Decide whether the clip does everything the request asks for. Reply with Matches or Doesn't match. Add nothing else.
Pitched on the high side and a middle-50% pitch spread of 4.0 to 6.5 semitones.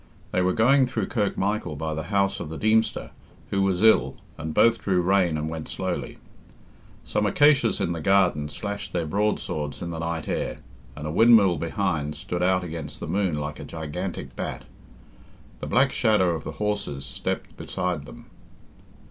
Doesn't match